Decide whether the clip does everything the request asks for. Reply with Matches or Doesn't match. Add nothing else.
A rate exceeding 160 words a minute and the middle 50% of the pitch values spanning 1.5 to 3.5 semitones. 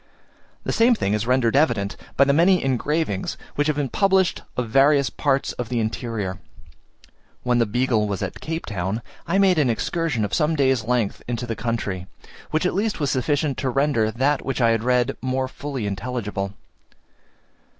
Doesn't match